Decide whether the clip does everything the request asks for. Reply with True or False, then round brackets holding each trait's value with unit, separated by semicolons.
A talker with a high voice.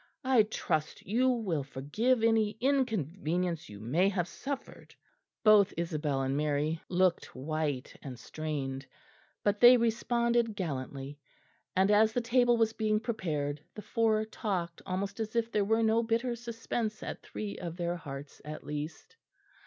True (200 Hz)